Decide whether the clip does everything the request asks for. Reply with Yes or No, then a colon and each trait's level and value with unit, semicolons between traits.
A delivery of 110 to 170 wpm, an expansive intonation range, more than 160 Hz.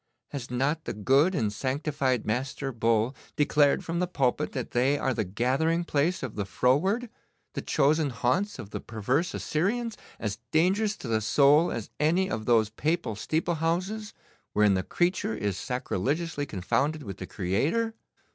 No: average, 160 wpm; wide, 6.6 semitones; medium, 140 Hz